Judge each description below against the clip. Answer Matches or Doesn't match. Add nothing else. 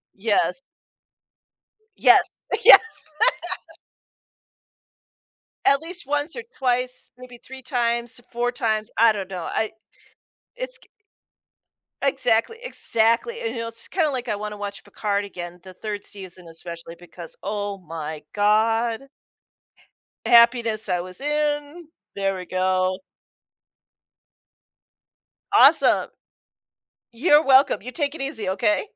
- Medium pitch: Doesn't match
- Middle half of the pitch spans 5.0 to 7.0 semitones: Matches